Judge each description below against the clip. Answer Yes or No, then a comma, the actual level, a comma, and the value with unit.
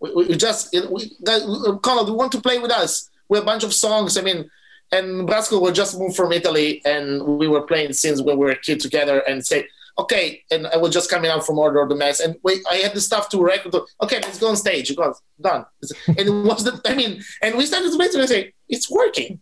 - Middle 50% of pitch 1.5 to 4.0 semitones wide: No, wide, 5.4 semitones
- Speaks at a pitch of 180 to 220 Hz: Yes, high, 190 Hz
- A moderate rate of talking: No, fast, 255 wpm